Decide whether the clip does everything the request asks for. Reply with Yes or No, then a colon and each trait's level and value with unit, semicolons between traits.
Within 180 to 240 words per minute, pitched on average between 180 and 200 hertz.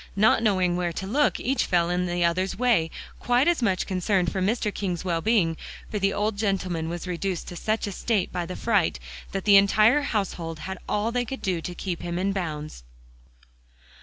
Yes: average, 200 wpm; high, 190 Hz